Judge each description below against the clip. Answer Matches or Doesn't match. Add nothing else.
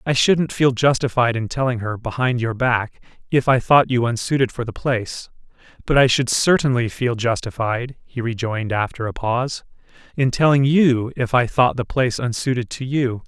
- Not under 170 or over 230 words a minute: Matches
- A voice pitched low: Matches